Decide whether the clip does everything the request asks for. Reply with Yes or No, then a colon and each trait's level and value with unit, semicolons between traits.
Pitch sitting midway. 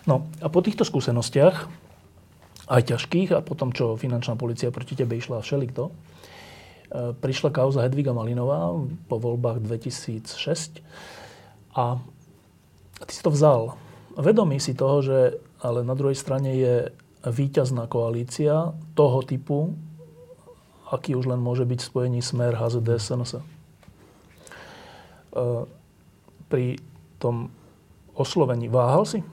No: low, 130 Hz